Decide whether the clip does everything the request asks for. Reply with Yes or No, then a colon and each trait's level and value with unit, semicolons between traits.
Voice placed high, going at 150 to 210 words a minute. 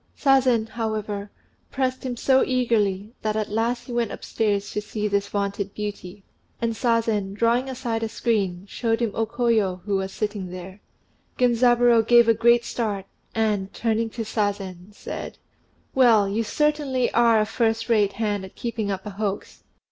Yes: high, 220 Hz; average, 165 wpm